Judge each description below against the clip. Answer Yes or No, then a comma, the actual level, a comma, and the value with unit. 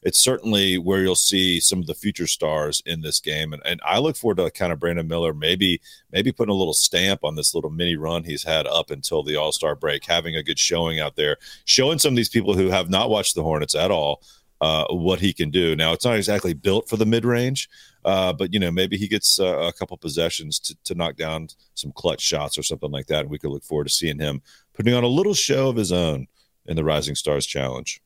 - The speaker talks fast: Yes, fast, 250 wpm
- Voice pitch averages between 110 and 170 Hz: No, very low, 85 Hz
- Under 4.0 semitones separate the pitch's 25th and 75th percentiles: No, average, 4.6 semitones